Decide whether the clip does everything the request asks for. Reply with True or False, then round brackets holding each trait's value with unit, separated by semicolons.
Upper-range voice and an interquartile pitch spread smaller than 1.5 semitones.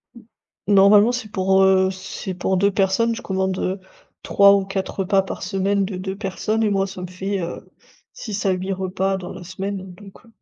True (195 Hz; 1.1 semitones)